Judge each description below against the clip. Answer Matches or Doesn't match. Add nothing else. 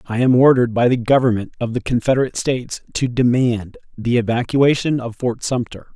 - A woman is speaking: Doesn't match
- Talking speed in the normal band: Matches